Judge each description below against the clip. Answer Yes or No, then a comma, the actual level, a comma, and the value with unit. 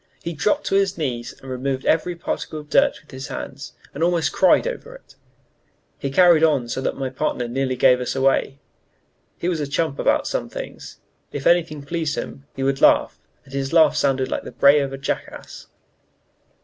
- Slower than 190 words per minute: No, average, 195 wpm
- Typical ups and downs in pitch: Yes, average, 3.8 semitones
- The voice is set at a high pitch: No, medium, 140 Hz